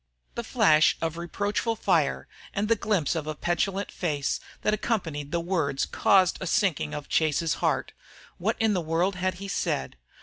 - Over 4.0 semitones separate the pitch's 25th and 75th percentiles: Yes, average, 4.4 semitones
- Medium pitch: Yes, medium, 175 Hz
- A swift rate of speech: No, average, 170 wpm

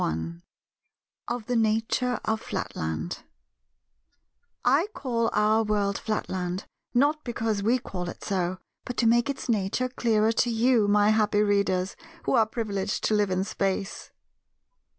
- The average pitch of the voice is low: No, high, 215 Hz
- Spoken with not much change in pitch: No, average, 3.2 semitones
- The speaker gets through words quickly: No, average, 145 wpm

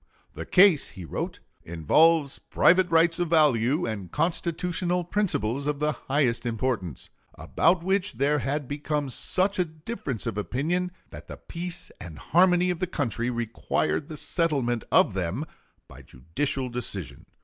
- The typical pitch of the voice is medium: Yes, medium, 150 Hz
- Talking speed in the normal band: Yes, average, 145 wpm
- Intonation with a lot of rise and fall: Yes, wide, 6.5 semitones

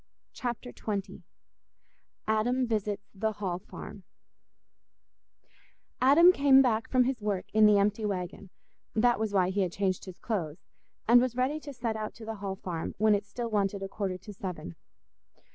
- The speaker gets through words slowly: No, average, 160 wpm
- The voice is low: No, high, 210 Hz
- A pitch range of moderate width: Yes, average, 3.6 semitones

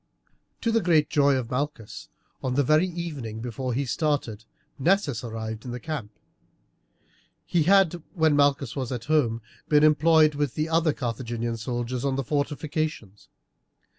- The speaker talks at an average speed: Yes, average, 150 wpm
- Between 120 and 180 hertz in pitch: Yes, medium, 140 Hz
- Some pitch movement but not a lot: Yes, average, 4.6 semitones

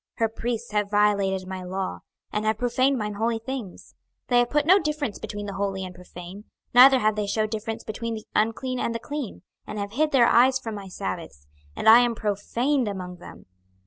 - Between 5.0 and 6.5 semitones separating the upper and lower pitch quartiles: No, average, 3.4 semitones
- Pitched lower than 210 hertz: No, high, 220 Hz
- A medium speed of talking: No, fast, 210 wpm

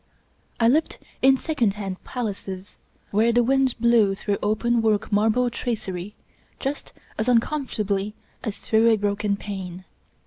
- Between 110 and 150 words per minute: Yes, slow, 135 wpm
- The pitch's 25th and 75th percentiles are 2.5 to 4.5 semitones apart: Yes, average, 3.0 semitones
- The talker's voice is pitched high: Yes, high, 220 Hz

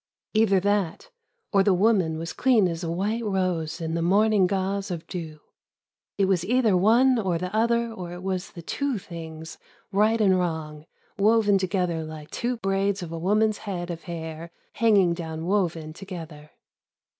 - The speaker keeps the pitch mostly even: No, average, 3.8 semitones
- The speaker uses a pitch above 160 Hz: Yes, medium, 185 Hz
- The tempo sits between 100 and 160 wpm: No, average, 170 wpm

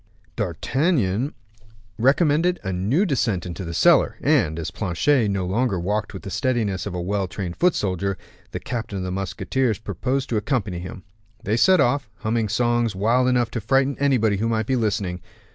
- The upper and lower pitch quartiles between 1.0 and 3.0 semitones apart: No, average, 5.3 semitones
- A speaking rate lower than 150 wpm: No, average, 180 wpm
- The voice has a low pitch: Yes, low, 110 Hz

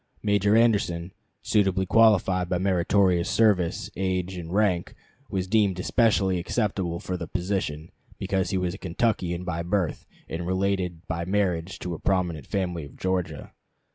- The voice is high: No, very low, 90 Hz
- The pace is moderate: Yes, average, 145 wpm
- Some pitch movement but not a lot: No, narrow, 2.3 semitones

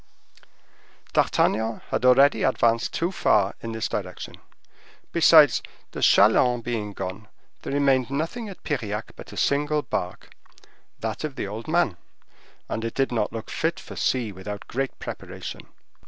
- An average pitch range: Yes, average, 4.9 semitones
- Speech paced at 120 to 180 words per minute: Yes, average, 140 wpm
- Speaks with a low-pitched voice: Yes, low, 120 Hz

